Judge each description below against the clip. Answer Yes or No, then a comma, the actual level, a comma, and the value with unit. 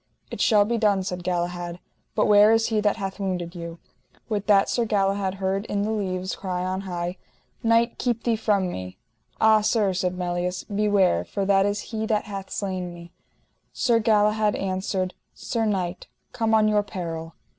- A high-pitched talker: Yes, high, 195 Hz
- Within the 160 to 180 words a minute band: Yes, average, 175 wpm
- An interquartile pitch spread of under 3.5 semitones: Yes, average, 2.8 semitones